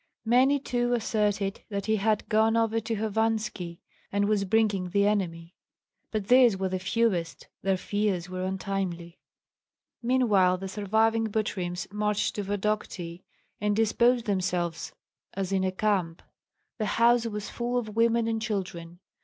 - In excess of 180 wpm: No, average, 145 wpm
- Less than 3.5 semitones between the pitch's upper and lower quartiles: Yes, average, 3.1 semitones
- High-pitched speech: Yes, high, 205 Hz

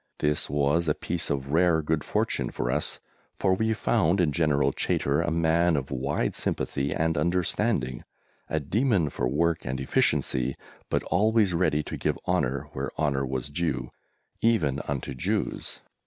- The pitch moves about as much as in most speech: Yes, average, 3.9 semitones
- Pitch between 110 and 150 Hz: No, very low, 75 Hz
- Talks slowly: No, average, 155 wpm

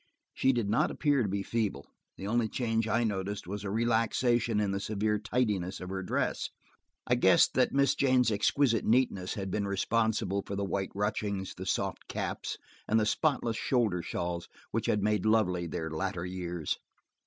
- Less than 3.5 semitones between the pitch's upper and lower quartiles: Yes, average, 3.1 semitones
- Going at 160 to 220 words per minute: Yes, average, 175 wpm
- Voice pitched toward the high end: No, low, 105 Hz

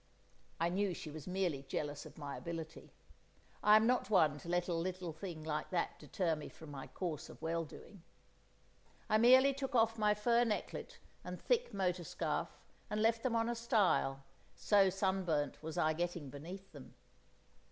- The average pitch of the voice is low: No, medium, 180 Hz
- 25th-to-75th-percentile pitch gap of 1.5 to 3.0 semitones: No, average, 5.2 semitones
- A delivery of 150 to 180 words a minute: Yes, average, 175 wpm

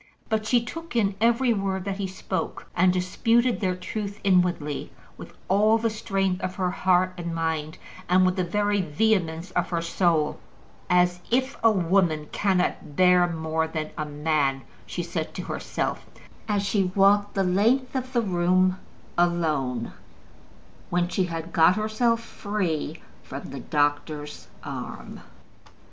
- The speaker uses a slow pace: No, average, 150 wpm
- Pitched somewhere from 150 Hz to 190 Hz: Yes, medium, 185 Hz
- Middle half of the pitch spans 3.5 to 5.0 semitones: Yes, average, 4.0 semitones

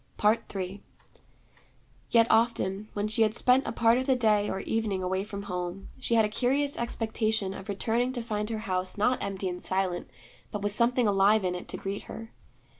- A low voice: No, high, 210 Hz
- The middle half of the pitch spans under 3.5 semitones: Yes, average, 2.9 semitones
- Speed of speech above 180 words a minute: Yes, average, 190 wpm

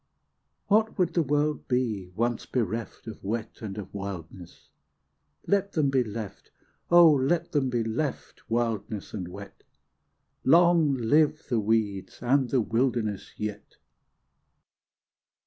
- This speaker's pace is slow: Yes, slow, 125 wpm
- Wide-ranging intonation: Yes, wide, 5.7 semitones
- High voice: No, low, 120 Hz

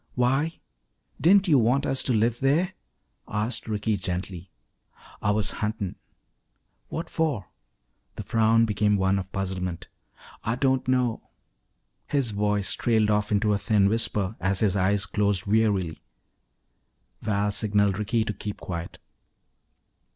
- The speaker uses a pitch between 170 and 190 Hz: No, low, 105 Hz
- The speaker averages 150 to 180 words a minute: No, slow, 135 wpm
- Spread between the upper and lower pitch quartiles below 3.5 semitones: Yes, average, 2.9 semitones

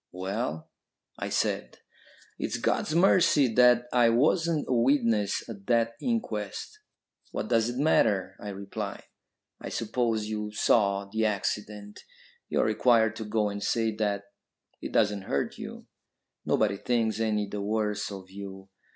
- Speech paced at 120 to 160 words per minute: Yes, average, 140 wpm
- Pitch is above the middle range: No, low, 110 Hz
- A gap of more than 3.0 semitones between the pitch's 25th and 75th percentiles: No, average, 2.7 semitones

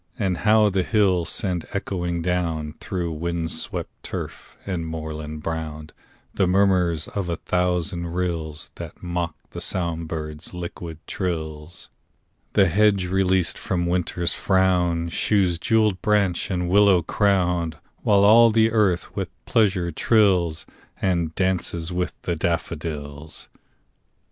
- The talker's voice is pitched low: Yes, very low, 90 Hz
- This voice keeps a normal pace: No, slow, 125 wpm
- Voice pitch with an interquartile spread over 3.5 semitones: No, narrow, 2.5 semitones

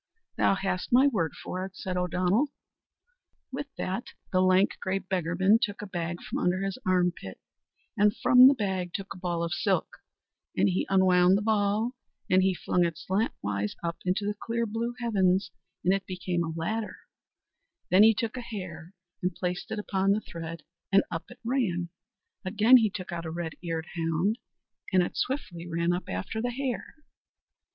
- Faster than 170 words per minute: Yes, average, 180 wpm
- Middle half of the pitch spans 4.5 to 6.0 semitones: No, average, 3.4 semitones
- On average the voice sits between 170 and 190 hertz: Yes, medium, 185 Hz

